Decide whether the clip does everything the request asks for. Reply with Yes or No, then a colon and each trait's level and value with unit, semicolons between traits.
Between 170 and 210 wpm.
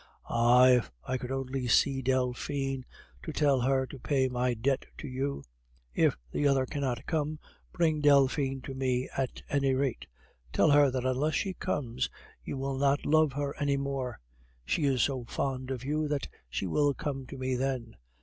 Yes: average, 180 wpm